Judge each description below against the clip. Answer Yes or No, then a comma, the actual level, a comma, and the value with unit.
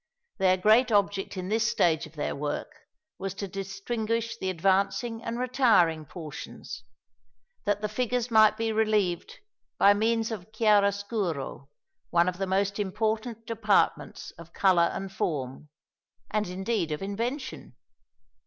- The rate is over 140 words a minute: No, slow, 135 wpm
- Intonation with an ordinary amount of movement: Yes, average, 3.7 semitones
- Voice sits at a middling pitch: No, high, 200 Hz